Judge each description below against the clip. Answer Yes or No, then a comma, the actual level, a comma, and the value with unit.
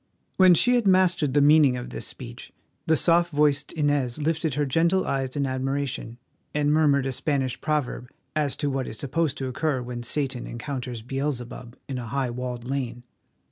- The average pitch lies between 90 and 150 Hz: Yes, medium, 140 Hz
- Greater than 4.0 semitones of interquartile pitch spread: No, average, 3.2 semitones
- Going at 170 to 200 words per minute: Yes, average, 180 wpm